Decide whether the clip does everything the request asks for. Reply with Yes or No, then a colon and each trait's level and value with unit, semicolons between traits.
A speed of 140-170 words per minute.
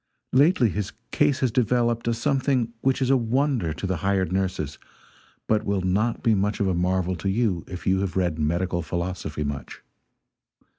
No: average, 185 wpm